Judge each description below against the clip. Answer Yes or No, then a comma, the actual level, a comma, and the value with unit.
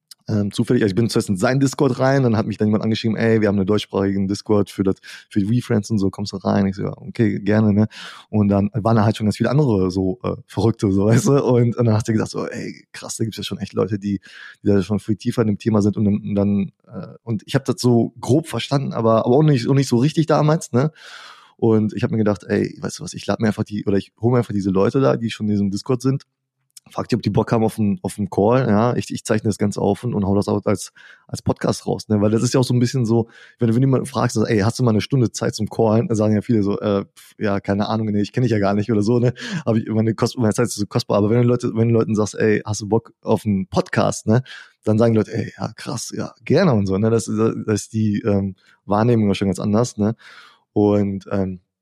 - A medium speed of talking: No, fast, 285 wpm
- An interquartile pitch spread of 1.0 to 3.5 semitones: Yes, average, 2.7 semitones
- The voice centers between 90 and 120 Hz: Yes, low, 110 Hz